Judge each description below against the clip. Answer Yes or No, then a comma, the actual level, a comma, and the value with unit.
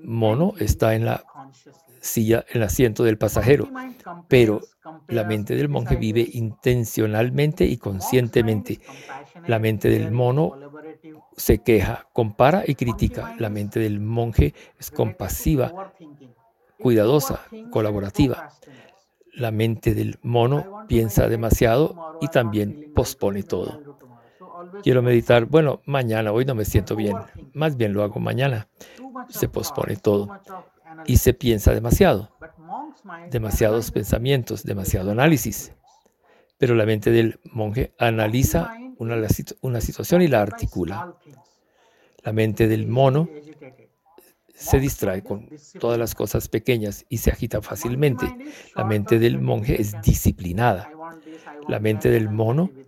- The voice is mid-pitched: No, low, 120 Hz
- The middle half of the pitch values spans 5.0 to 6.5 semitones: Yes, average, 5.3 semitones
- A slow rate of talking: Yes, slow, 125 wpm